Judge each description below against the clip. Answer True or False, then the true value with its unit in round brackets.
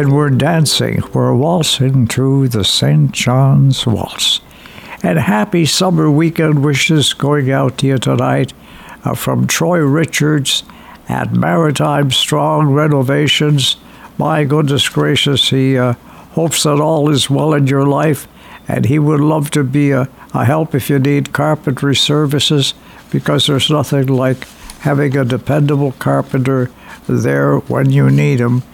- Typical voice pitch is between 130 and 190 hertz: True (140 Hz)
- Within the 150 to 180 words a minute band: False (140 wpm)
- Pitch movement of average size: False (2.1 semitones)